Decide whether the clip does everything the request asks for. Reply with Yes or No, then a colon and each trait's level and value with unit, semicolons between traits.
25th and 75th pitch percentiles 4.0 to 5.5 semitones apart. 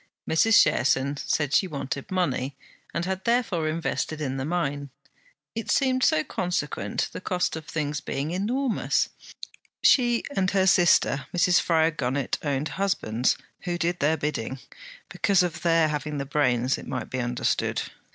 Yes: average, 4.7 semitones